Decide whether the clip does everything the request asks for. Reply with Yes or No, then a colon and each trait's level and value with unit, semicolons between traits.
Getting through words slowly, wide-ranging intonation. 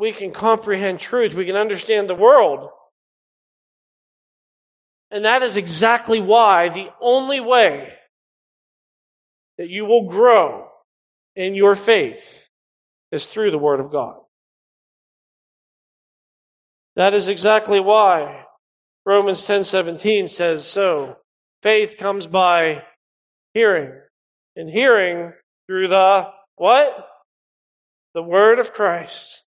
No: slow, 105 wpm; average, 3.1 semitones